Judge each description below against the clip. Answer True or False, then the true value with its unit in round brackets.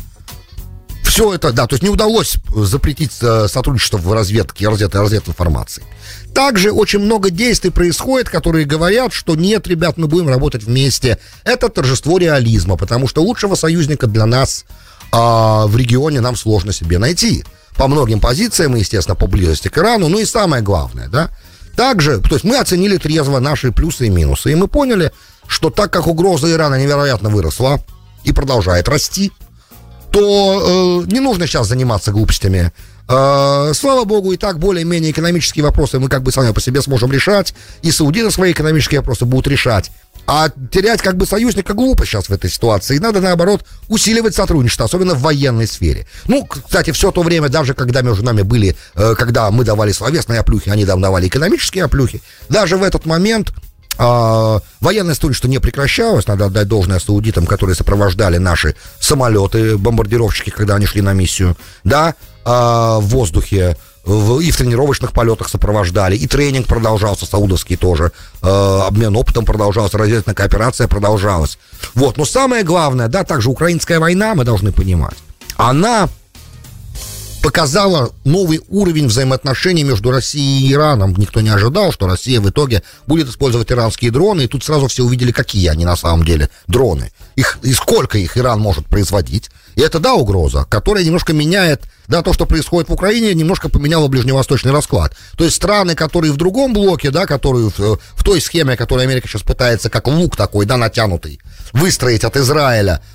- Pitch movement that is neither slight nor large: False (7.9 semitones)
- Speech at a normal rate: True (165 wpm)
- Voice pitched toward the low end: True (125 Hz)